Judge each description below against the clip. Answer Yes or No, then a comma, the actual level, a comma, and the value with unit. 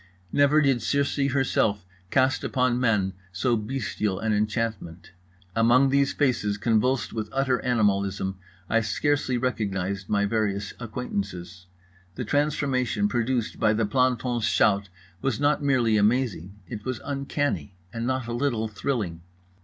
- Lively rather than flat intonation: No, average, 4.2 semitones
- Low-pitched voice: Yes, low, 115 Hz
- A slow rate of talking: Yes, slow, 130 wpm